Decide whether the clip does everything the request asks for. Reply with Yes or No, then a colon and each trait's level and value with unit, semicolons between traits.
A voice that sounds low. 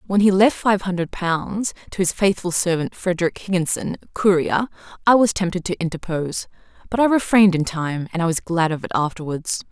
No: medium, 180 Hz